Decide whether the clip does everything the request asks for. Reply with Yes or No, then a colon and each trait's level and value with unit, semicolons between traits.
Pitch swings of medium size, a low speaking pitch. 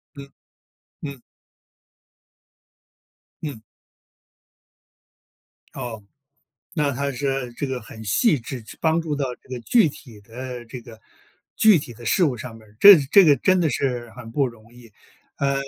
Yes: average, 3.6 semitones; low, 130 Hz